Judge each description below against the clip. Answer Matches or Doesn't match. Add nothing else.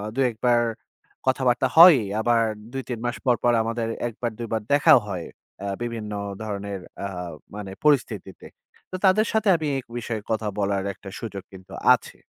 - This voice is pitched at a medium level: Doesn't match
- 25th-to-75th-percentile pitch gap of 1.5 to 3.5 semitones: Doesn't match